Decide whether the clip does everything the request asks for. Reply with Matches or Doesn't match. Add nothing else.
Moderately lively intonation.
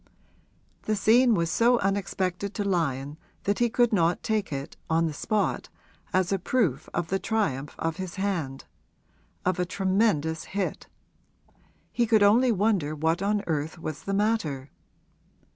Matches